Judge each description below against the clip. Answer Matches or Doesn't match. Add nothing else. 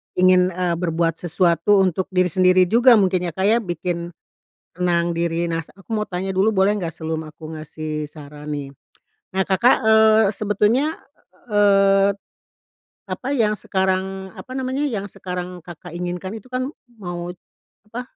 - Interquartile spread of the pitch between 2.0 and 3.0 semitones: Doesn't match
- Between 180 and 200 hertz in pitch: Matches